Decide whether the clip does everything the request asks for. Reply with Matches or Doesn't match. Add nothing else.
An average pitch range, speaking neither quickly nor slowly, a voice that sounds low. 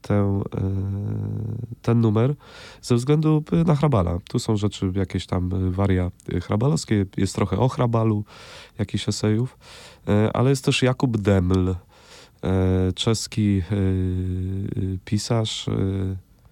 Doesn't match